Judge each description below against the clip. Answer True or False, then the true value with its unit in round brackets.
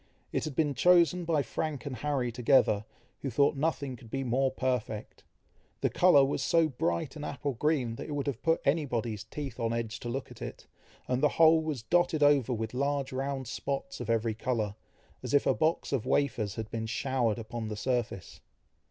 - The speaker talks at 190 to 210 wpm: True (200 wpm)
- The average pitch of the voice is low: True (130 Hz)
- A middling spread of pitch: True (4.0 semitones)